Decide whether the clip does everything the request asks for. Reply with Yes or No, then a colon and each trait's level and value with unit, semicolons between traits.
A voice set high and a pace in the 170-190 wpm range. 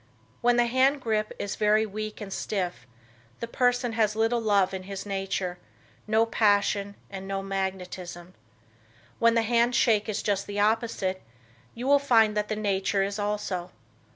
No: high, 210 Hz; average, 160 wpm